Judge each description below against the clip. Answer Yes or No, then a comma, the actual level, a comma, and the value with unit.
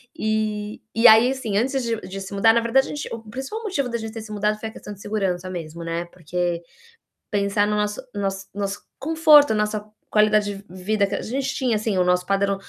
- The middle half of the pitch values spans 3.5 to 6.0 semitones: No, average, 2.8 semitones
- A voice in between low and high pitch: No, high, 210 Hz